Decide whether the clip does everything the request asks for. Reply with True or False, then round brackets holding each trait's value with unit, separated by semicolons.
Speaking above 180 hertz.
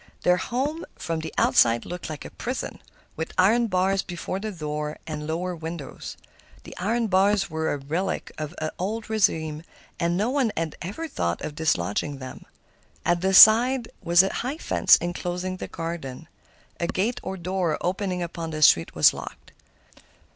False (175 Hz)